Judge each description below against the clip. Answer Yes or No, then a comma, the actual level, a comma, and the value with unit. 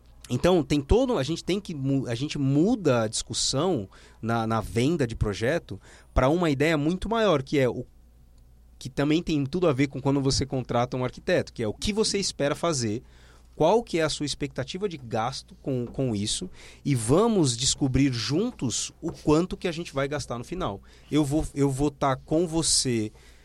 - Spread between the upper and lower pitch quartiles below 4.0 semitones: No, wide, 5.5 semitones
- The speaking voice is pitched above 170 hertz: No, medium, 140 Hz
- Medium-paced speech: No, fast, 190 wpm